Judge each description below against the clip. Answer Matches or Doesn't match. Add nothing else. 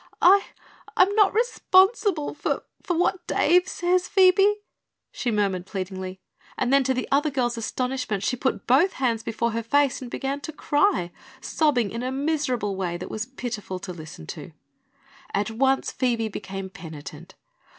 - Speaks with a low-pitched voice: Doesn't match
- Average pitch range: Doesn't match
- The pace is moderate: Matches